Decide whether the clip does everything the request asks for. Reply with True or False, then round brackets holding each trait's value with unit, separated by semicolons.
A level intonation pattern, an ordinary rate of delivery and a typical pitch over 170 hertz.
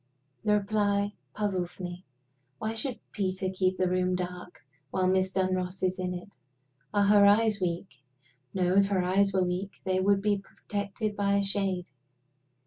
True (1.7 semitones; 160 wpm; 190 Hz)